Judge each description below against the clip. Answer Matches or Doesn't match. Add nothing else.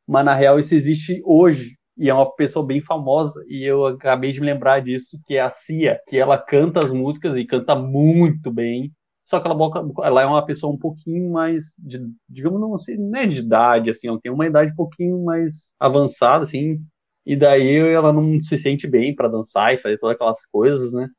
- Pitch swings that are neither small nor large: Matches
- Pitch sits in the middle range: Matches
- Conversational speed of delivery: Doesn't match